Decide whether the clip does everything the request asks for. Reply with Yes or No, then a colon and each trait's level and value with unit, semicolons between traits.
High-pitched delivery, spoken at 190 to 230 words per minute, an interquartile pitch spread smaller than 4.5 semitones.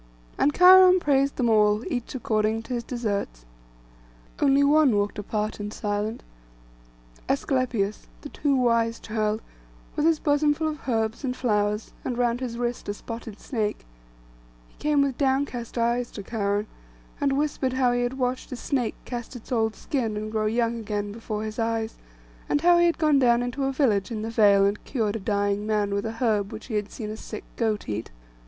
Yes: high, 230 Hz; average, 195 wpm; average, 3.8 semitones